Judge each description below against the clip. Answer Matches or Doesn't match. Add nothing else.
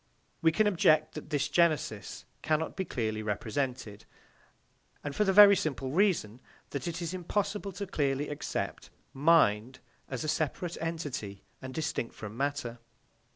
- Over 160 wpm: Doesn't match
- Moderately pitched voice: Matches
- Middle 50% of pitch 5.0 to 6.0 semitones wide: Matches